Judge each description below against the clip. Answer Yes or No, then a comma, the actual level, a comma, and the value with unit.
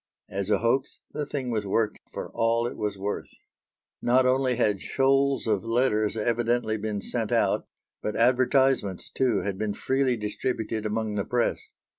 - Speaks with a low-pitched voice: Yes, low, 115 Hz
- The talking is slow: No, average, 160 wpm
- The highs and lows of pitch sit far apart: No, average, 3.3 semitones